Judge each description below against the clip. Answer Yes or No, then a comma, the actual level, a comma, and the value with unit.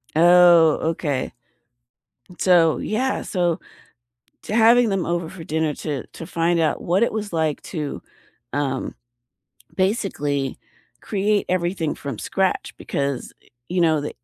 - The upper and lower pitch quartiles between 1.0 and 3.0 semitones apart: No, average, 3.7 semitones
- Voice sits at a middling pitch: Yes, medium, 170 Hz